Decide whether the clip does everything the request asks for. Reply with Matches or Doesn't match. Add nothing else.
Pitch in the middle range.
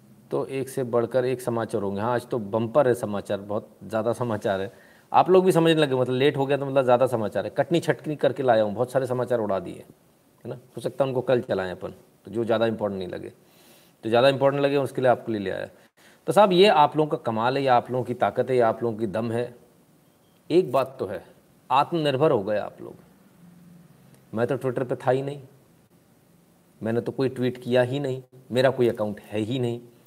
Doesn't match